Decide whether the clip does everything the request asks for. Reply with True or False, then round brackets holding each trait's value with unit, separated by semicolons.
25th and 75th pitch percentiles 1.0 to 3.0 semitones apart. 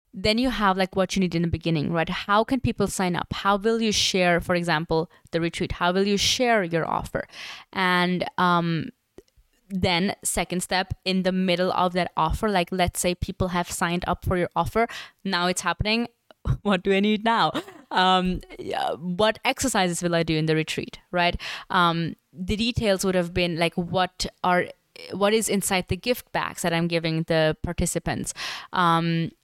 True (2.5 semitones)